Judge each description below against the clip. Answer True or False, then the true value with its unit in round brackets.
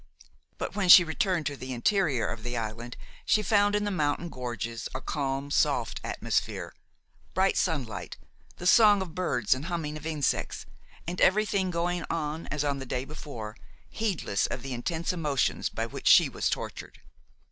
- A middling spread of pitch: False (6.0 semitones)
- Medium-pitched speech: True (155 Hz)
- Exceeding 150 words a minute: True (170 wpm)